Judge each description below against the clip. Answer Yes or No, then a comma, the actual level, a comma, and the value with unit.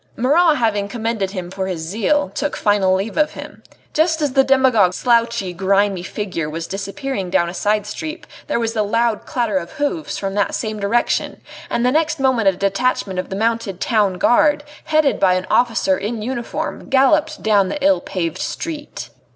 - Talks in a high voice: Yes, high, 220 Hz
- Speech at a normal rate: Yes, average, 185 wpm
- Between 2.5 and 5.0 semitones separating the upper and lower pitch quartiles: No, wide, 5.5 semitones